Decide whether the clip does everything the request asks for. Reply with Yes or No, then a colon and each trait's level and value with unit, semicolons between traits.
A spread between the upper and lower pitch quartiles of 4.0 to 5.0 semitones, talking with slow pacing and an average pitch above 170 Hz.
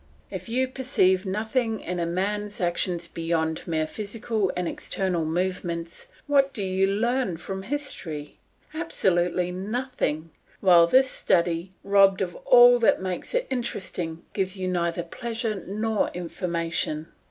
Yes: average, 4.6 semitones; slow, 130 wpm; high, 190 Hz